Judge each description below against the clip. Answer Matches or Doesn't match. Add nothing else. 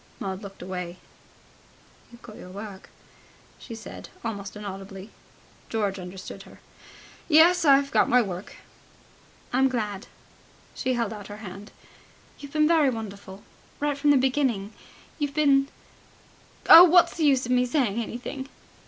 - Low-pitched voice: Doesn't match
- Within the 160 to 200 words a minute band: Doesn't match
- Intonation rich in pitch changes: Matches